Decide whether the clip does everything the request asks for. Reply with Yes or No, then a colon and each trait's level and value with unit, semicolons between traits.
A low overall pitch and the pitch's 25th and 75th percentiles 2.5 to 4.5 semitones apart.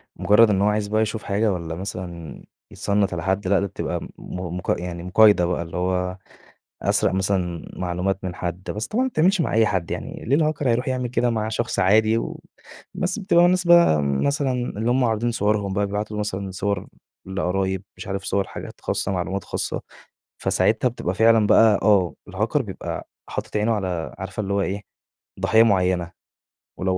Yes: low, 100 Hz; average, 3.5 semitones